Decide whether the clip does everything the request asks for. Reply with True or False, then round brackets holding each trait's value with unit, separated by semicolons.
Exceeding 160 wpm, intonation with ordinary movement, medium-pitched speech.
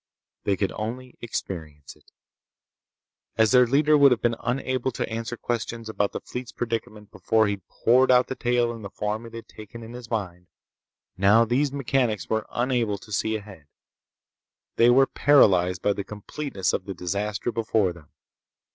False (170 wpm; 3.3 semitones; 115 Hz)